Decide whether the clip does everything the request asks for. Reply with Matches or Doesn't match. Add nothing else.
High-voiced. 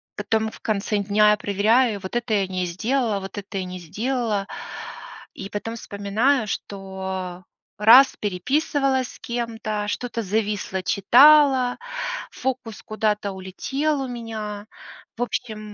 Matches